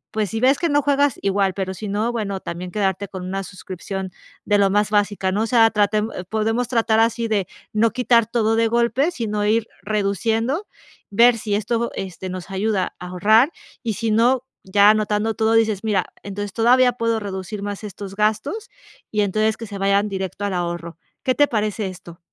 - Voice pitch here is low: No, high, 210 Hz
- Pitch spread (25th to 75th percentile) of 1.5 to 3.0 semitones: Yes, narrow, 2.6 semitones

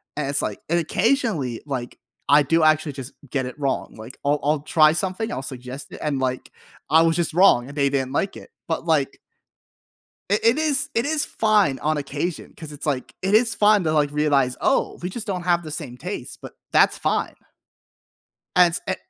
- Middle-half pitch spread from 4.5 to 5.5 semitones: Yes, average, 4.9 semitones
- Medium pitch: Yes, medium, 155 Hz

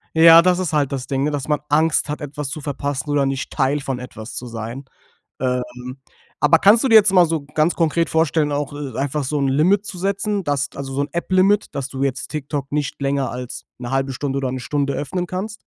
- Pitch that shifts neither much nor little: Yes, average, 3.5 semitones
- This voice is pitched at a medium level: Yes, medium, 145 Hz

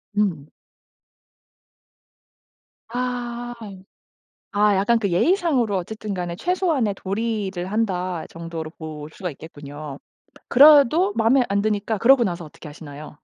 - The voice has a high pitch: Yes, high, 205 Hz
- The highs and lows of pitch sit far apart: Yes, wide, 5.8 semitones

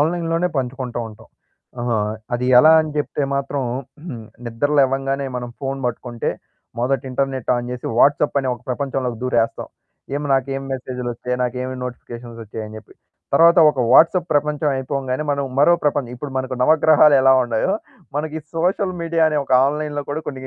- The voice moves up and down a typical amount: Yes, average, 3.1 semitones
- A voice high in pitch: No, low, 135 Hz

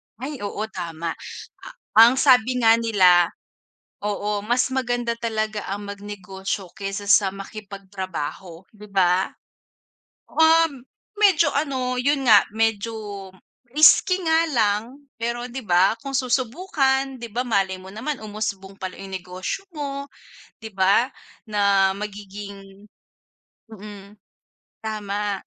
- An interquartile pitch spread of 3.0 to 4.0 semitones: No, average, 4.4 semitones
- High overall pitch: Yes, high, 210 Hz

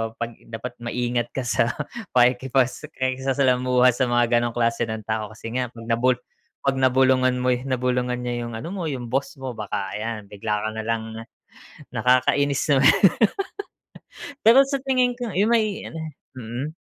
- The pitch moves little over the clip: Yes, narrow, 2.3 semitones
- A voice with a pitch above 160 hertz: No, low, 125 Hz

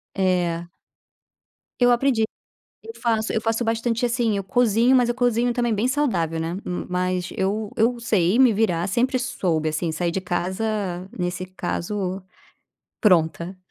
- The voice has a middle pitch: No, high, 210 Hz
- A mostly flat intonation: No, average, 5.0 semitones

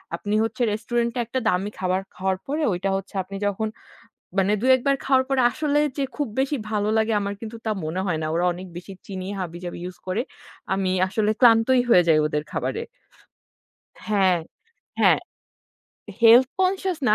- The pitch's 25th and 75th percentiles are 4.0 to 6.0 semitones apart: Yes, average, 5.1 semitones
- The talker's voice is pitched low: No, high, 210 Hz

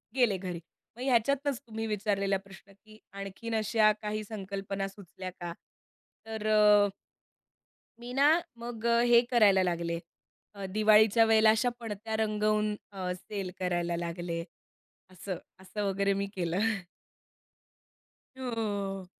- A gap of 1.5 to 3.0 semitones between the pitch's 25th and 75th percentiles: Yes, narrow, 2.5 semitones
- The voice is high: Yes, high, 210 Hz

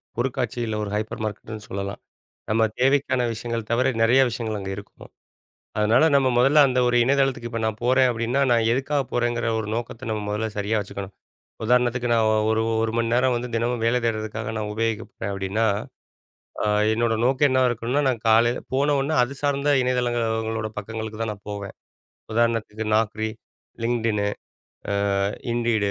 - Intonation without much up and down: Yes, narrow, 2.3 semitones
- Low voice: Yes, low, 115 Hz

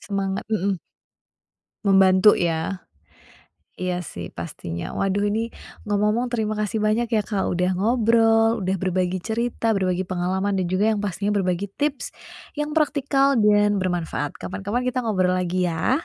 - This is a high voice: Yes, high, 200 Hz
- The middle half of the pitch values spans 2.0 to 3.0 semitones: No, average, 3.4 semitones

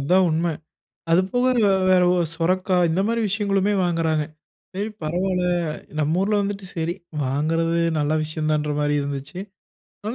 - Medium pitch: Yes, medium, 170 Hz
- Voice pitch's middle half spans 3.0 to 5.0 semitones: Yes, average, 3.8 semitones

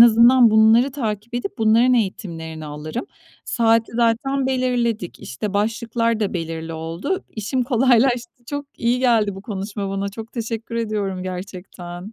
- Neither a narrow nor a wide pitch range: Yes, average, 3.6 semitones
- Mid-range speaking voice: No, high, 225 Hz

